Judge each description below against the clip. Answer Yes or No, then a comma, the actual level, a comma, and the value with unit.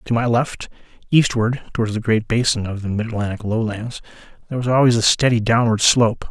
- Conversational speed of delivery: Yes, average, 190 wpm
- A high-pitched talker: No, low, 115 Hz